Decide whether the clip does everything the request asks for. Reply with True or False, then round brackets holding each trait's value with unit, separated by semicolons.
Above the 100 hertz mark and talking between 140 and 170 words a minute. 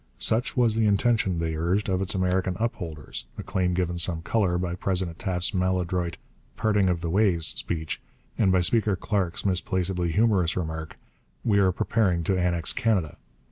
False (90 Hz; 165 wpm)